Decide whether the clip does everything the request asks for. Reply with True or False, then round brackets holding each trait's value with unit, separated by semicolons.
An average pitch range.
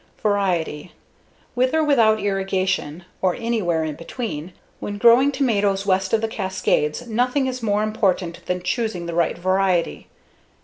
True (4.3 semitones)